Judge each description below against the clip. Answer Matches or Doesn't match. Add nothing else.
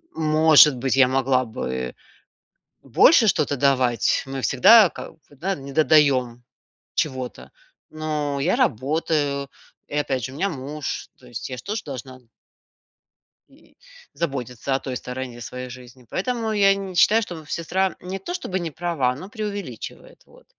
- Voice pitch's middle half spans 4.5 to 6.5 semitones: Matches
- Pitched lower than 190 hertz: Matches